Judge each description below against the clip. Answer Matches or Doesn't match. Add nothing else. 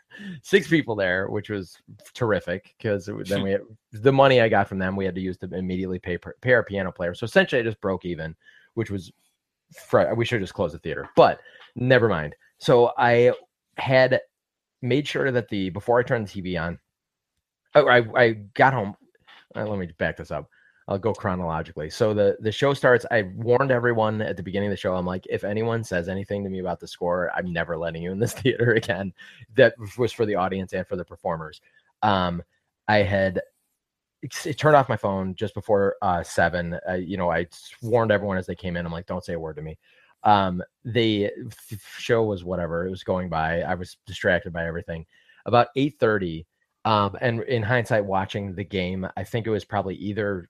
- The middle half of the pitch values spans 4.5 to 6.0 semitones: Doesn't match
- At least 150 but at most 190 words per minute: Doesn't match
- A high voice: Doesn't match